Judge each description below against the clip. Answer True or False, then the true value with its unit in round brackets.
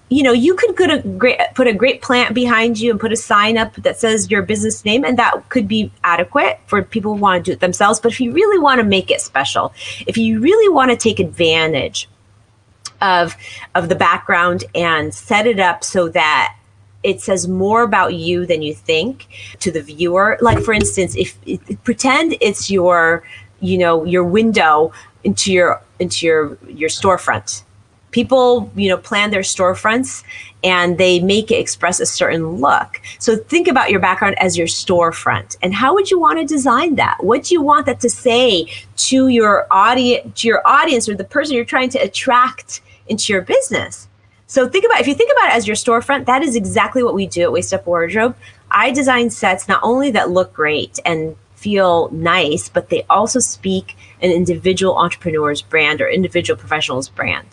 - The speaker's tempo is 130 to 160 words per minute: False (195 wpm)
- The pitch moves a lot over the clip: True (6.1 semitones)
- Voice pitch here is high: True (200 Hz)